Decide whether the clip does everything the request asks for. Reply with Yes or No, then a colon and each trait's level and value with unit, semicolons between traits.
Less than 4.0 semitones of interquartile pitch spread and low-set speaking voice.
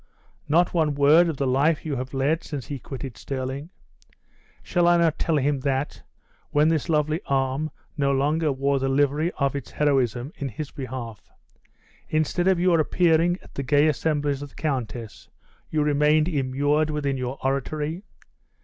No: narrow, 2.5 semitones; medium, 145 Hz